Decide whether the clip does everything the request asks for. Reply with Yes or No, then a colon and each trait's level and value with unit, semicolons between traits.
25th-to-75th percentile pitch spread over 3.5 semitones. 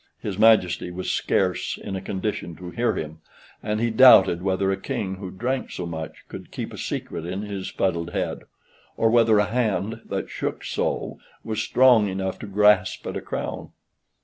No: average, 3.1 semitones